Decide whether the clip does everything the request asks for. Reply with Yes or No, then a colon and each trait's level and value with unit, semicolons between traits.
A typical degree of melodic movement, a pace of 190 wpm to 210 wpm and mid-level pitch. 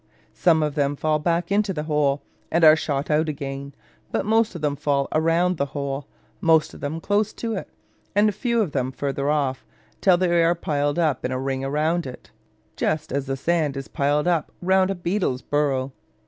Yes: average, 3.7 semitones; average, 200 wpm; medium, 150 Hz